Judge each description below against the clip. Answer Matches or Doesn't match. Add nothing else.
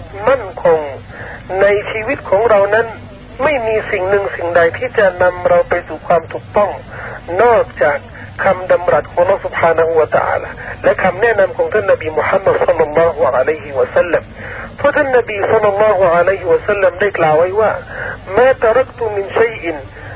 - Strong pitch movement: Matches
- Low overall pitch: Doesn't match